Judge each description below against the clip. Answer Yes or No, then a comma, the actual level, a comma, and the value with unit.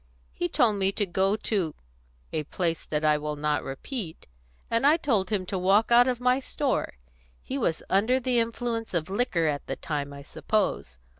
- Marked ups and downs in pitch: Yes, wide, 7.1 semitones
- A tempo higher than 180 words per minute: Yes, average, 190 wpm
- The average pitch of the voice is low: No, high, 195 Hz